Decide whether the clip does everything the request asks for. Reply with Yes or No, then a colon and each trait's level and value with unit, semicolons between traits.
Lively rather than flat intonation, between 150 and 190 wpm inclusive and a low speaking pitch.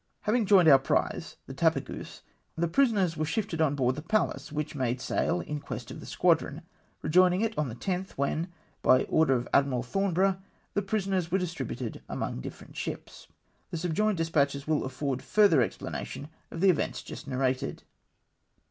No: wide, 5.7 semitones; average, 180 wpm; medium, 160 Hz